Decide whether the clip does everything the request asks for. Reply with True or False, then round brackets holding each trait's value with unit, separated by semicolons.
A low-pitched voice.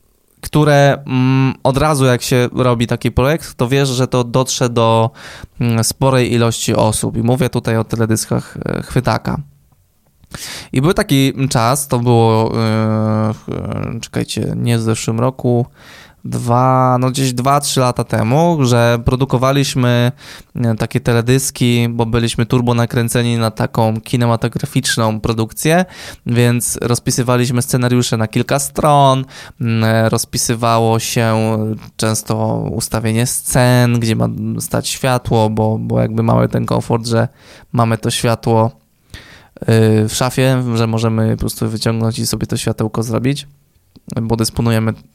True (120 Hz)